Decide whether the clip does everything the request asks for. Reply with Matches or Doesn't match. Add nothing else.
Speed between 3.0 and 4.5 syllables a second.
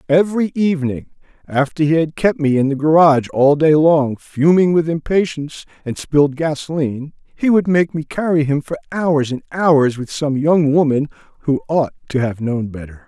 Doesn't match